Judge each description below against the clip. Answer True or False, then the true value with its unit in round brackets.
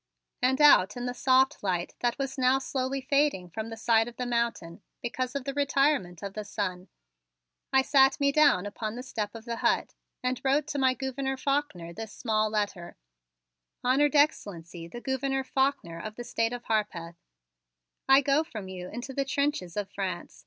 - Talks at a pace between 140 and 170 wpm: False (180 wpm)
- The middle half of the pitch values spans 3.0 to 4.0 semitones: False (4.7 semitones)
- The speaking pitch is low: False (245 Hz)